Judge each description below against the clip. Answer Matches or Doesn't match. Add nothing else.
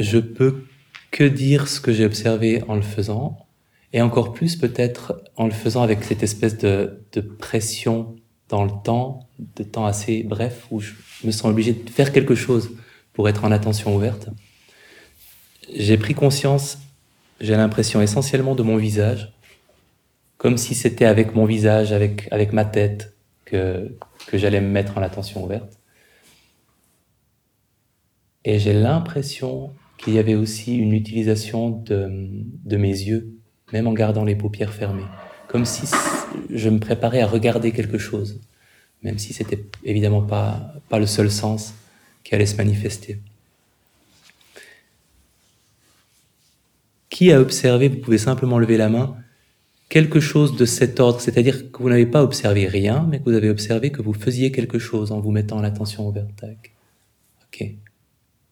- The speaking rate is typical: Matches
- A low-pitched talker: Matches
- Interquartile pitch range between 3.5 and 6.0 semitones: Doesn't match